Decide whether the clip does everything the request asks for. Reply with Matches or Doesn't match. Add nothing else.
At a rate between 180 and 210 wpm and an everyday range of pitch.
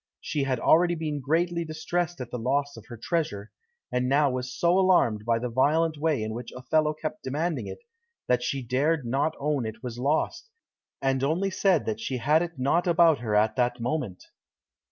Matches